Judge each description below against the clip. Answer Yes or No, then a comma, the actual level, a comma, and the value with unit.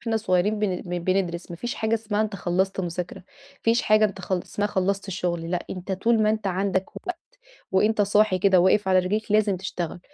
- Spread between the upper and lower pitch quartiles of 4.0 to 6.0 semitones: No, average, 2.8 semitones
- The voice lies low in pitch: No, high, 195 Hz